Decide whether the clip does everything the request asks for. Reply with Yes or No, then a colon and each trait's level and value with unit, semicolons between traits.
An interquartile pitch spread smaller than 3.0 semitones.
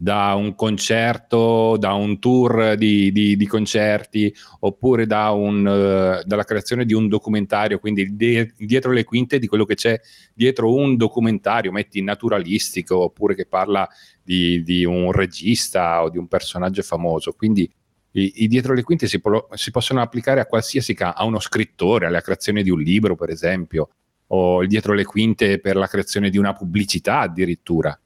Yes: narrow, 2.6 semitones